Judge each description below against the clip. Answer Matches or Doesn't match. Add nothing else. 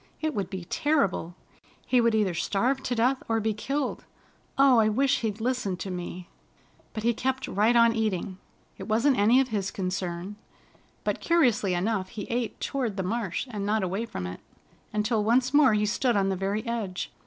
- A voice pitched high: Matches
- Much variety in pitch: Doesn't match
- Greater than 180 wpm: Matches